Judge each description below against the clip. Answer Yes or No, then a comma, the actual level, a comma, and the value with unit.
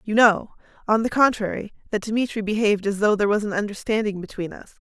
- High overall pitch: Yes, high, 210 Hz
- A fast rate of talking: No, average, 195 wpm